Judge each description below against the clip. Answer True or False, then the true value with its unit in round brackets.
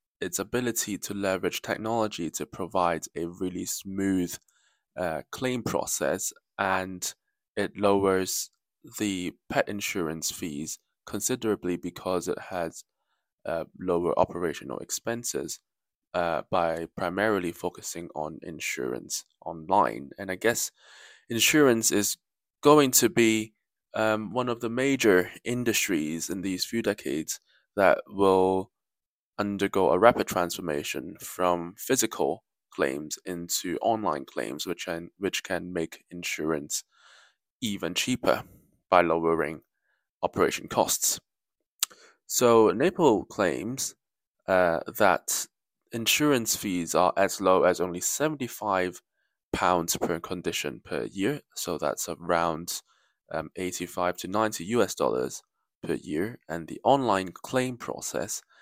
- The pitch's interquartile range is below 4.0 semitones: False (4.3 semitones)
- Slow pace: True (115 wpm)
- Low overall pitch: True (95 Hz)